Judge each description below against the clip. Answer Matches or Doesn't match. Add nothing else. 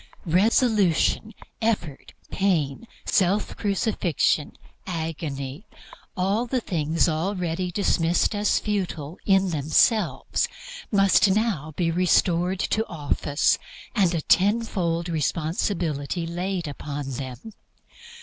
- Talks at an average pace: Doesn't match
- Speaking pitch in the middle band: Matches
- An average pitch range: Matches